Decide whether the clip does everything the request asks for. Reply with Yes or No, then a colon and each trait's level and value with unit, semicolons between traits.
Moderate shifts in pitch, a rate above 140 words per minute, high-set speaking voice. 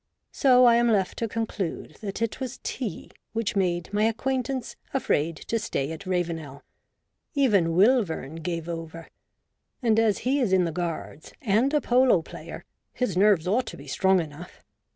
No: wide, 6.0 semitones; average, 165 wpm; high, 200 Hz